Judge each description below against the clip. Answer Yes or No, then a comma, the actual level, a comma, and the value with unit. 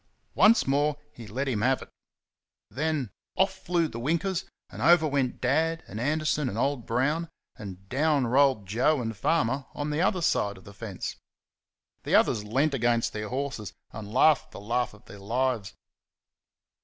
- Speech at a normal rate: Yes, average, 170 wpm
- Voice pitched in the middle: No, low, 130 Hz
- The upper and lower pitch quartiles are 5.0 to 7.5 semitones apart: Yes, wide, 5.5 semitones